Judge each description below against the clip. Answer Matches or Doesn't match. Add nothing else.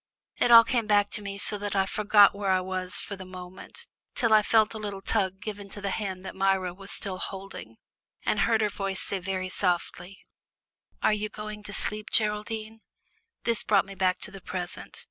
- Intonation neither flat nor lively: Doesn't match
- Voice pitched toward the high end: Matches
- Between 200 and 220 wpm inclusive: Matches